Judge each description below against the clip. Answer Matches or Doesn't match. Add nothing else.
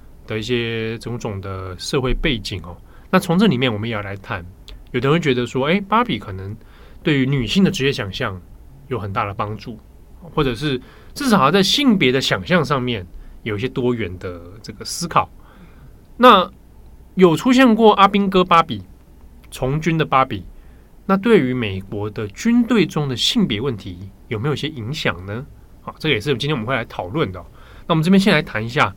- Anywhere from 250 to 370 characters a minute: Matches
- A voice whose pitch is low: Matches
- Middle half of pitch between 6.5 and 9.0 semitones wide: Matches